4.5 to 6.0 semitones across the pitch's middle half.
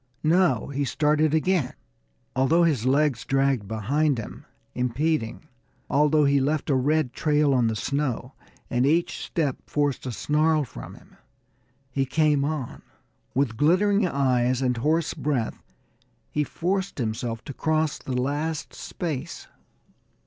No: average, 3.5 semitones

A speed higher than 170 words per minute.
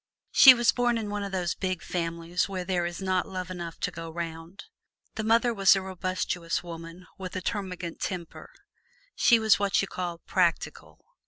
Yes: average, 180 wpm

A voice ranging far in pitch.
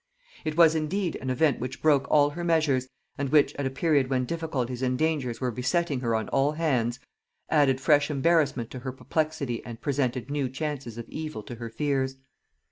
No: average, 3.5 semitones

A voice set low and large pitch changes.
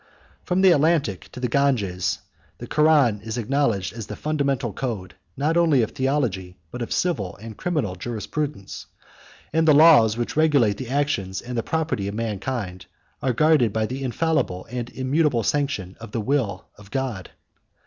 Yes: low, 125 Hz; wide, 5.9 semitones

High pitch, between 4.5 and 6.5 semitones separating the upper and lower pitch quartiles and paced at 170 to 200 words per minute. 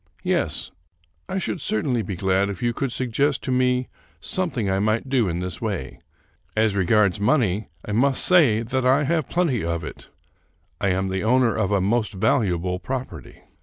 No: low, 110 Hz; average, 5.2 semitones; average, 180 wpm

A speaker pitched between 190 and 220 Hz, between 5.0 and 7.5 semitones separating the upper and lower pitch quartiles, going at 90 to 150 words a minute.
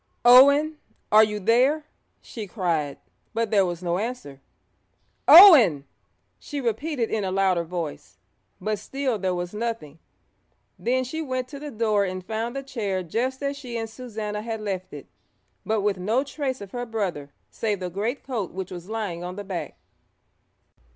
No: high, 215 Hz; average, 5.3 semitones; average, 165 wpm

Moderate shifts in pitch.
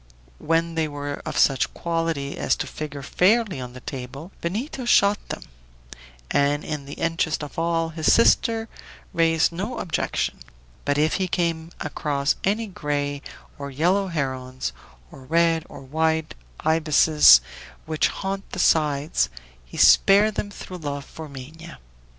Yes: average, 3.2 semitones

